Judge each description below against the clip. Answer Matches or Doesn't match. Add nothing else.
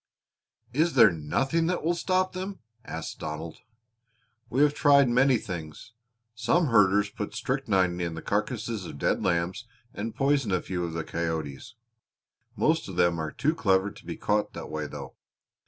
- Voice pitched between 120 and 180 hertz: Doesn't match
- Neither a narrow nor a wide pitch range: Doesn't match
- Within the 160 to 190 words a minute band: Matches